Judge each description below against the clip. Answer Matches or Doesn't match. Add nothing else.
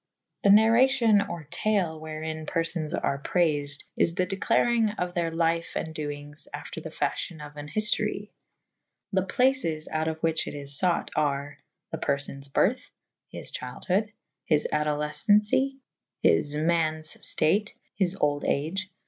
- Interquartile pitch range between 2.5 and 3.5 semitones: Doesn't match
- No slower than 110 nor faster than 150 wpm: Matches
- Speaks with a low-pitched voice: Doesn't match